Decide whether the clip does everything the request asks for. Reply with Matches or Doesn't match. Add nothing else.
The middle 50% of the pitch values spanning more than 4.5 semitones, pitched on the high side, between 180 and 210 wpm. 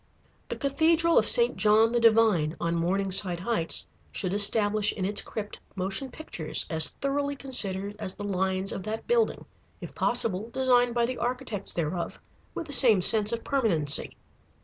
Doesn't match